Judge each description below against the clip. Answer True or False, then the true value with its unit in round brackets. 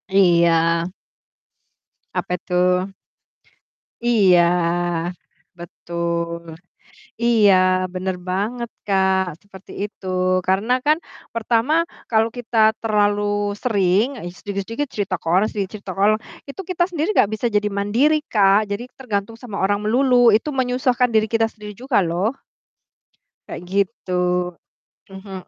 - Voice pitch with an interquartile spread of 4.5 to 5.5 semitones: False (3.6 semitones)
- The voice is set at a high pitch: True (205 Hz)